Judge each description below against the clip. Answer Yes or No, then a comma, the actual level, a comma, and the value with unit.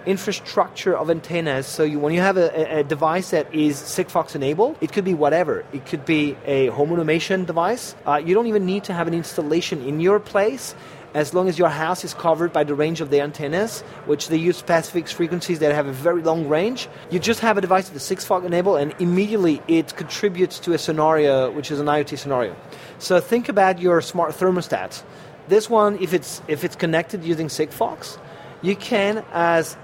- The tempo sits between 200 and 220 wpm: Yes, fast, 205 wpm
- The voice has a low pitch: No, medium, 170 Hz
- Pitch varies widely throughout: No, average, 3.6 semitones